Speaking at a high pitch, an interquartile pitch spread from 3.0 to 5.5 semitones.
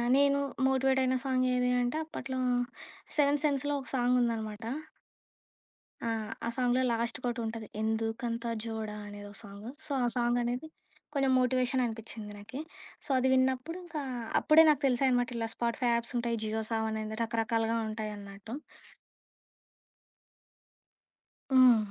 No: high, 240 Hz; narrow, 2.6 semitones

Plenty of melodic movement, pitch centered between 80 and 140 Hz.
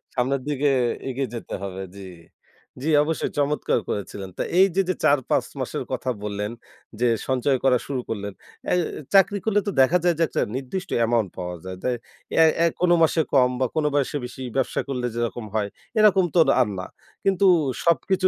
Yes: wide, 6.4 semitones; low, 135 Hz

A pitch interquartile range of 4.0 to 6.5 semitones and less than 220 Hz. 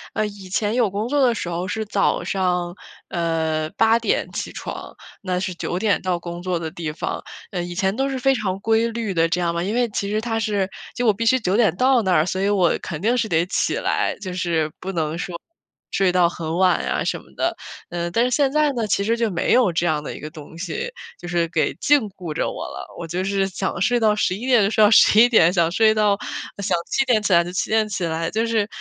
Yes: average, 4.4 semitones; high, 195 Hz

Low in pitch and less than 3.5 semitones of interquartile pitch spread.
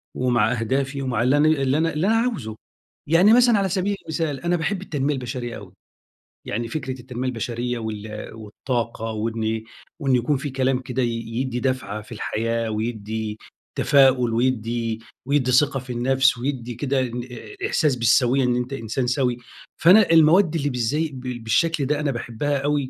No: low, 130 Hz; average, 3.8 semitones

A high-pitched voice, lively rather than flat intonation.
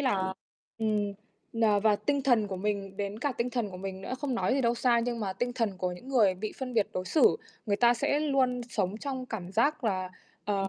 No: high, 220 Hz; average, 4.2 semitones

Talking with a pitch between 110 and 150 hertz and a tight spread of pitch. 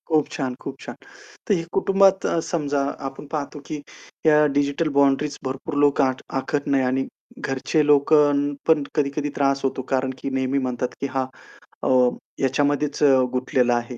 Yes: medium, 140 Hz; narrow, 2.0 semitones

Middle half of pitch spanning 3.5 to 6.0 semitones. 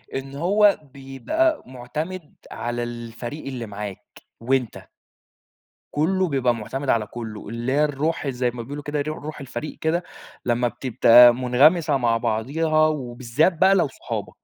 Yes: average, 4.4 semitones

